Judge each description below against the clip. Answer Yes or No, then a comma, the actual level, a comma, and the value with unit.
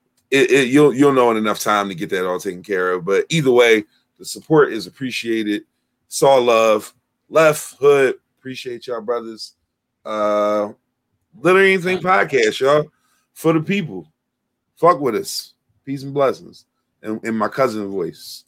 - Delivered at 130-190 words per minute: Yes, average, 155 wpm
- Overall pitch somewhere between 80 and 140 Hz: Yes, low, 135 Hz